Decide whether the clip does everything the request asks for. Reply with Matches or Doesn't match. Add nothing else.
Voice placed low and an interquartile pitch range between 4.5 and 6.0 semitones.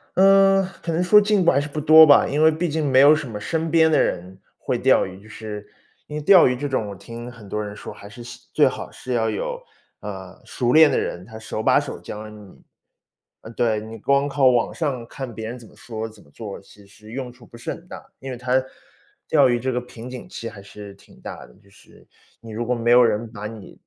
Matches